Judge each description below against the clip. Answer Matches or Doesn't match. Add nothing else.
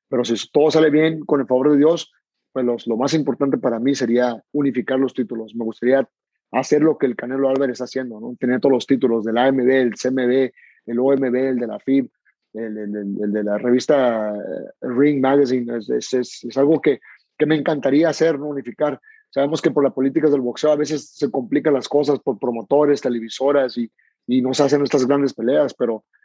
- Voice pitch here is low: Matches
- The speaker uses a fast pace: Matches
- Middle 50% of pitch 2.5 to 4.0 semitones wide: Matches